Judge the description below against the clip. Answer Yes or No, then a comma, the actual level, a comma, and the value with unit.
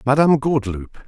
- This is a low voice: Yes, low, 130 Hz